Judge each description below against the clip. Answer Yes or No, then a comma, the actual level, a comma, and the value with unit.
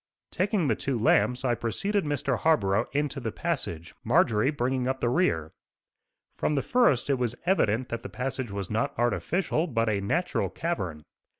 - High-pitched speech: No, low, 125 Hz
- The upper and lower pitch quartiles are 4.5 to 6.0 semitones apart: Yes, wide, 5.4 semitones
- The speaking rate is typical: Yes, average, 170 wpm